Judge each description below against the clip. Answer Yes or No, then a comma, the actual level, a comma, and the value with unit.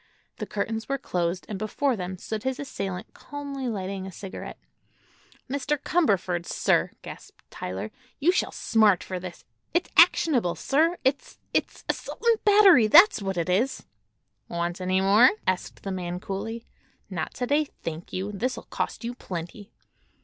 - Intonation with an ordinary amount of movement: No, wide, 6.6 semitones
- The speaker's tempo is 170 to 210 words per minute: No, average, 150 wpm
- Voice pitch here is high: Yes, high, 205 Hz